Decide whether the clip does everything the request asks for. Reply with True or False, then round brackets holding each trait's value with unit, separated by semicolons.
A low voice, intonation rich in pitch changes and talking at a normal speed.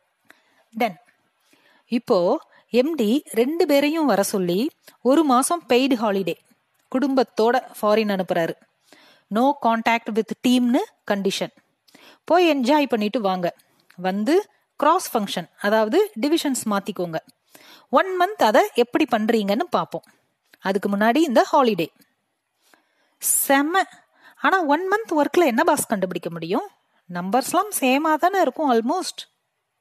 False (255 Hz; 6.6 semitones; 105 wpm)